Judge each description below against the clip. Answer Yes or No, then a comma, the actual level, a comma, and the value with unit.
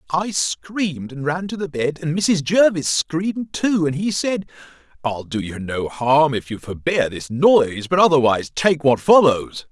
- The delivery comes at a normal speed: Yes, average, 185 wpm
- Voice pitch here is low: No, medium, 155 Hz